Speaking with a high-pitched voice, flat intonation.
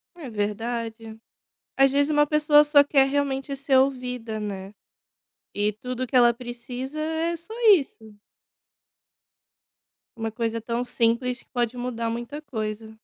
No: high, 245 Hz; average, 3.7 semitones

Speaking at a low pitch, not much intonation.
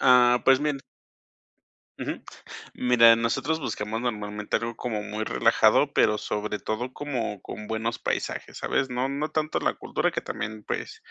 No: low, 115 Hz; average, 3.3 semitones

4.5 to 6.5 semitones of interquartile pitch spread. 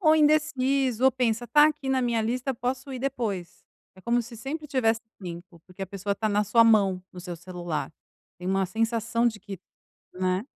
Yes: average, 5.2 semitones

